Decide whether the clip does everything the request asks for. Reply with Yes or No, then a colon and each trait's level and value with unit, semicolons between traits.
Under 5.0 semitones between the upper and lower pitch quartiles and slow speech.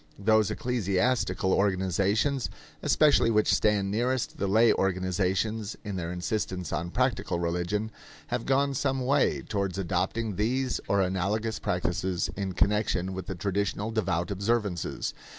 Yes: average, 3.4 semitones; slow, 130 wpm